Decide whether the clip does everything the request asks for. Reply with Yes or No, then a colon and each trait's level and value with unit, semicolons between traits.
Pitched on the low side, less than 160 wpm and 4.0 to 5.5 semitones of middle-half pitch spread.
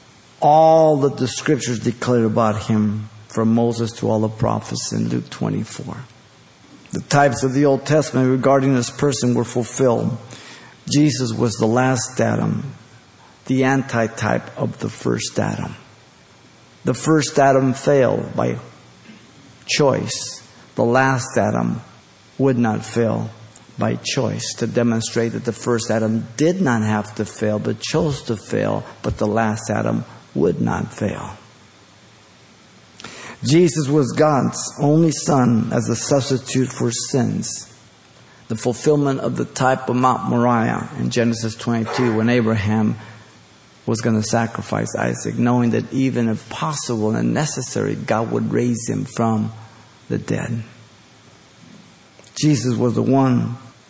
No: low, 120 Hz; slow, 135 wpm; average, 3.1 semitones